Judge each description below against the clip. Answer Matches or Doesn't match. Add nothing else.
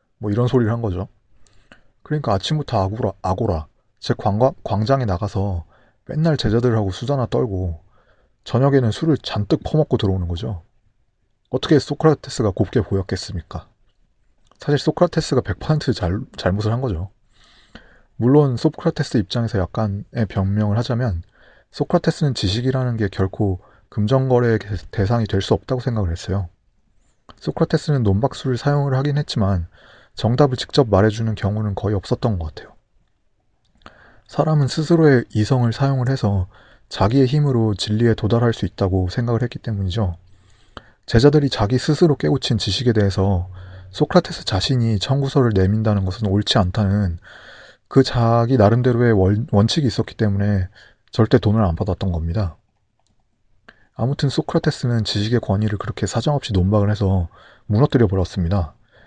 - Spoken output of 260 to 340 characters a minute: Matches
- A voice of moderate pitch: Doesn't match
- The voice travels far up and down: Doesn't match